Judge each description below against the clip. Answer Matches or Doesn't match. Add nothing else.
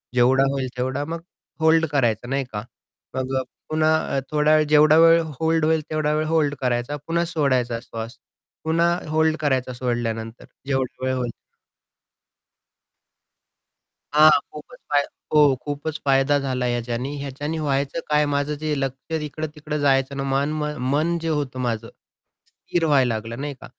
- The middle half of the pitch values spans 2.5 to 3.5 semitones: Matches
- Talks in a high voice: Doesn't match